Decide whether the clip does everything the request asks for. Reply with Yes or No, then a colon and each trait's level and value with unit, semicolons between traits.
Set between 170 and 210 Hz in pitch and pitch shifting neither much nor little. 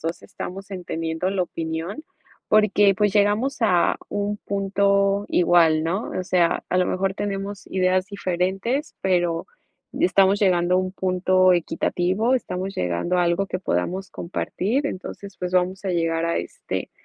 No: medium, 185 Hz; narrow, 2.2 semitones